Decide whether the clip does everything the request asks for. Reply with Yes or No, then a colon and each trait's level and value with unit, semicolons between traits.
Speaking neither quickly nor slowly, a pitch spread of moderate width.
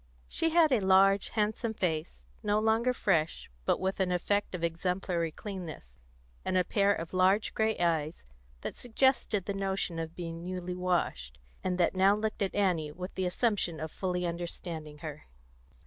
Yes: average, 165 wpm; average, 3.4 semitones